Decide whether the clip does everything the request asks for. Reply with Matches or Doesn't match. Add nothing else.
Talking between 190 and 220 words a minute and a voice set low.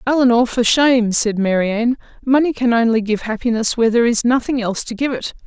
Doesn't match